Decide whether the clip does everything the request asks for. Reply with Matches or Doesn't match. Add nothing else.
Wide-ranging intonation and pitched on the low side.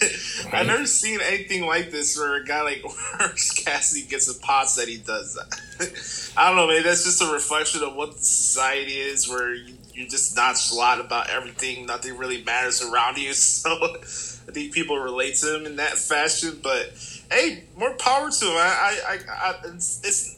Doesn't match